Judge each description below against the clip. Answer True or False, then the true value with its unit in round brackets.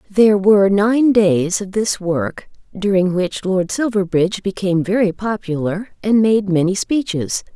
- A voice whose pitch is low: False (195 Hz)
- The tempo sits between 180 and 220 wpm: False (145 wpm)